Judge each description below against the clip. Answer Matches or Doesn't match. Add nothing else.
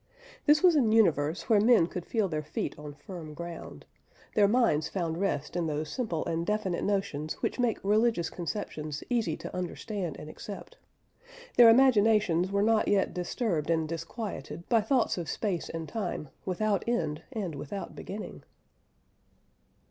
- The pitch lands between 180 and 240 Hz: Matches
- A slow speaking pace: Doesn't match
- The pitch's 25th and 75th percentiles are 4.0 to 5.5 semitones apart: Matches